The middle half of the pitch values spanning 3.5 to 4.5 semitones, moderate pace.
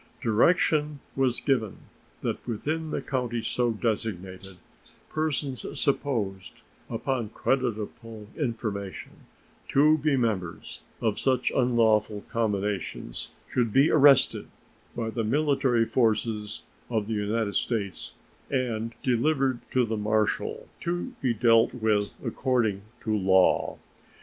No: average, 3.8 semitones; slow, 110 wpm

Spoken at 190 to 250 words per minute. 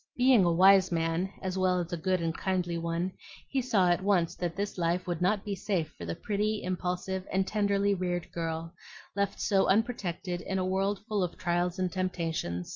Yes: average, 200 wpm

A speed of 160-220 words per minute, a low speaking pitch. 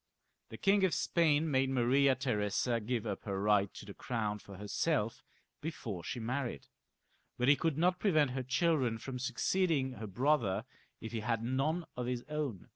Yes: average, 175 wpm; low, 125 Hz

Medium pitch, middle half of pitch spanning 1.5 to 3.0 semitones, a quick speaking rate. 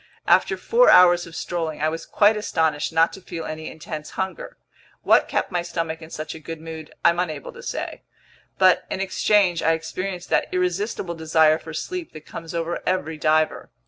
No: medium, 165 Hz; narrow, 2.5 semitones; average, 185 wpm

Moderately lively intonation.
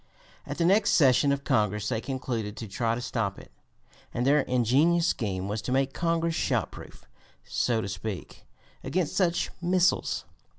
No: wide, 7.1 semitones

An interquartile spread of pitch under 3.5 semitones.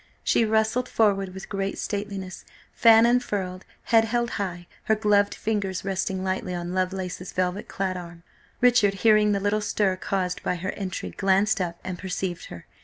Yes: narrow, 2.5 semitones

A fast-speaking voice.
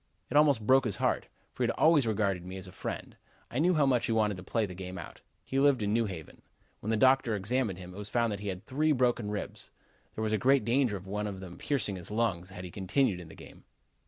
Yes: fast, 260 wpm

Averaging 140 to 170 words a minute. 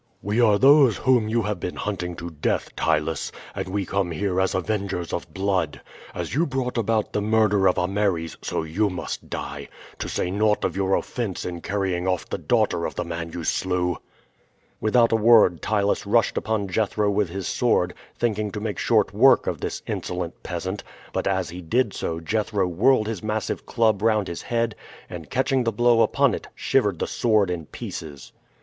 No: average, 190 wpm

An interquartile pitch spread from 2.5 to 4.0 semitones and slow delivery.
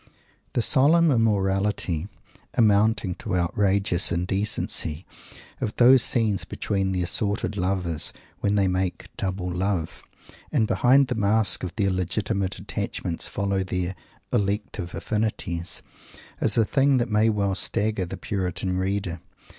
Yes: average, 2.9 semitones; slow, 125 wpm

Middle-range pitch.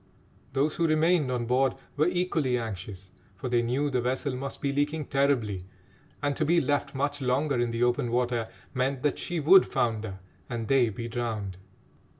No: low, 130 Hz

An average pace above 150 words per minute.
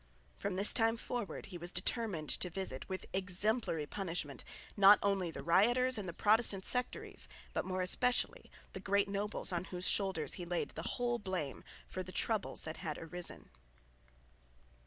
Yes: average, 160 wpm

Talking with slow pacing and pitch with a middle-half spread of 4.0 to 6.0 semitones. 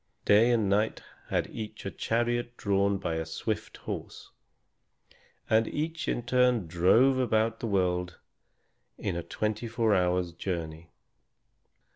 Yes: slow, 130 wpm; average, 4.8 semitones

